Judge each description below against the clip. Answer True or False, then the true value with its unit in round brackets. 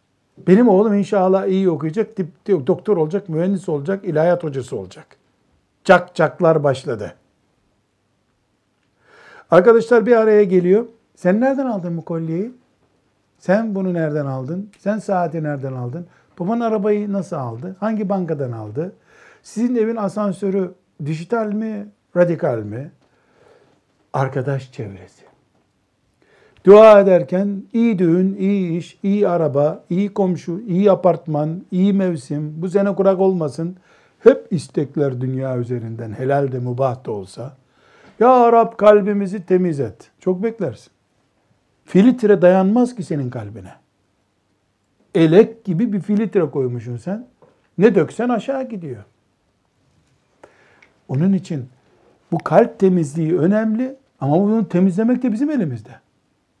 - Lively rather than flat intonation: True (6.6 semitones)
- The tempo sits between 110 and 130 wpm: True (120 wpm)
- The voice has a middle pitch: True (180 Hz)